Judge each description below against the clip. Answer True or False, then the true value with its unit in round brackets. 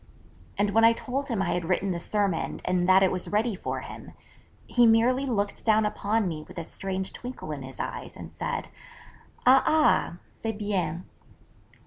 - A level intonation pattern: False (3.8 semitones)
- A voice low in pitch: False (205 Hz)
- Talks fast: False (185 wpm)